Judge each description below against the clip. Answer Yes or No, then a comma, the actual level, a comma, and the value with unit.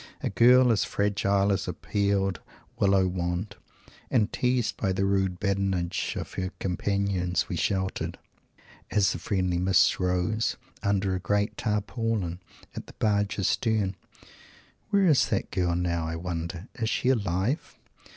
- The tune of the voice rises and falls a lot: No, narrow, 2.5 semitones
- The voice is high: No, low, 100 Hz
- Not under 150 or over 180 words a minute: No, average, 140 wpm